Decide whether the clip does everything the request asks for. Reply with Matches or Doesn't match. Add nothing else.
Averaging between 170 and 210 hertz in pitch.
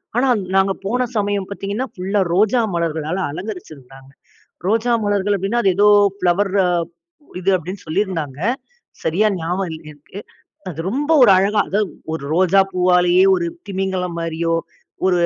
Matches